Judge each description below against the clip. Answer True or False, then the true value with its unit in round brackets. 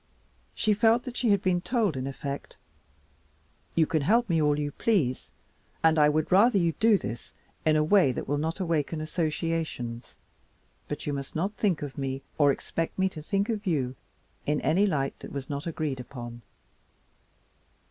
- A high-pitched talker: False (155 Hz)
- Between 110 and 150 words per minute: False (180 wpm)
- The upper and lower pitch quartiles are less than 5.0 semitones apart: False (5.3 semitones)